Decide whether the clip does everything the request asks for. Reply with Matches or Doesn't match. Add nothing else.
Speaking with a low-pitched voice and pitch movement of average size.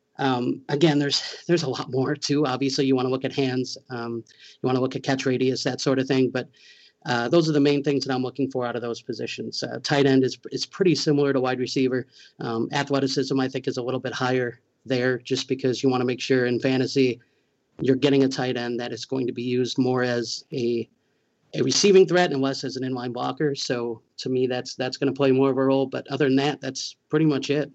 Doesn't match